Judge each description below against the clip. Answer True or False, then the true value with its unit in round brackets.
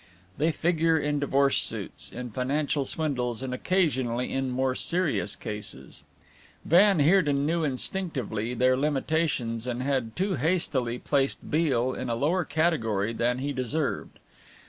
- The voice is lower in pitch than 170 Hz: True (140 Hz)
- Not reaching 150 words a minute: True (135 wpm)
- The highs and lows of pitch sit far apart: False (4.2 semitones)